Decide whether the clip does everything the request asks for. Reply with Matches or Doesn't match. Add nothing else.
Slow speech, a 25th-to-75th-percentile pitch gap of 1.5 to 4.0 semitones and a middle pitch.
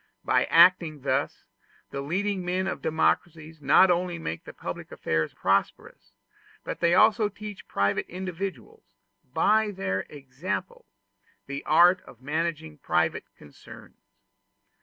Doesn't match